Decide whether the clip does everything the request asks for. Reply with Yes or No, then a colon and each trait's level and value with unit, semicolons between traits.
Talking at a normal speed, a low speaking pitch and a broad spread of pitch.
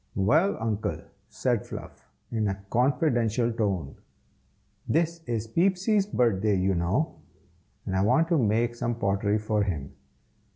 No: slow, 130 wpm; low, 115 Hz; wide, 6.3 semitones